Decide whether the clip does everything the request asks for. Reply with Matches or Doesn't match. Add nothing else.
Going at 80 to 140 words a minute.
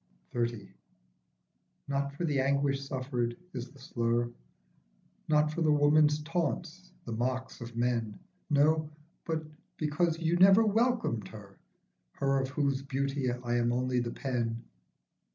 Matches